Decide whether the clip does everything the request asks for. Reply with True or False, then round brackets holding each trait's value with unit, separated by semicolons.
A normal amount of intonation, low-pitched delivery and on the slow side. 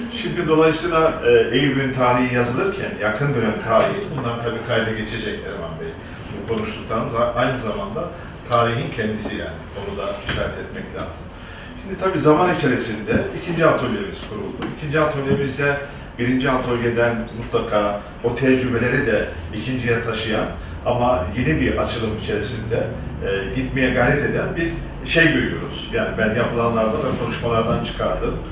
False (4.3 semitones; 120 Hz; 130 wpm)